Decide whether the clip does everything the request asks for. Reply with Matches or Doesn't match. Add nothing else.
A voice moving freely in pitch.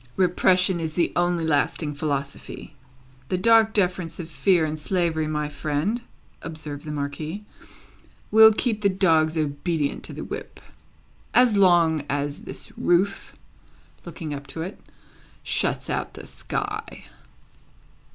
Doesn't match